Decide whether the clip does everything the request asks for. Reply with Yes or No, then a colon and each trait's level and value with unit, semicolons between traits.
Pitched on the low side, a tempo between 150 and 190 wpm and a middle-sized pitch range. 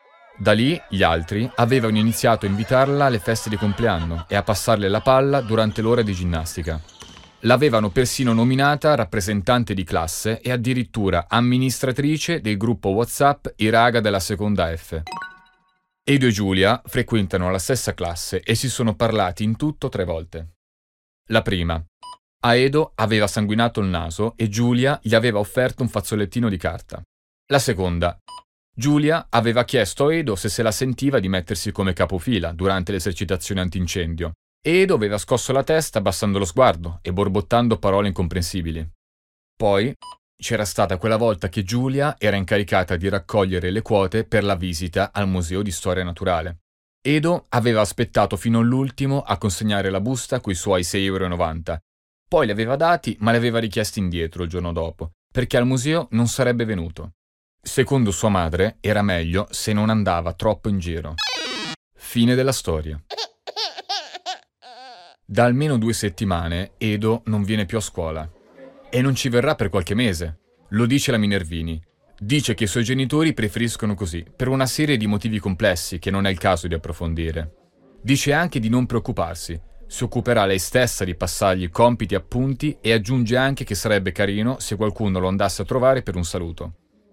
Yes: low, 105 Hz; average, 160 wpm; average, 5.0 semitones